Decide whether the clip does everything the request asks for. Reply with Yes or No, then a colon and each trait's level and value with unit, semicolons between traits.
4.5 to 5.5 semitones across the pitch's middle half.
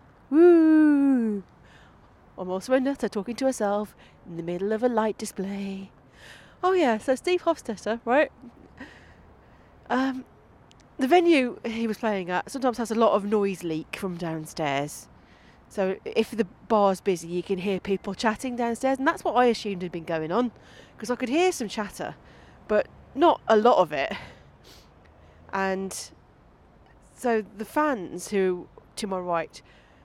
Yes: average, 5.2 semitones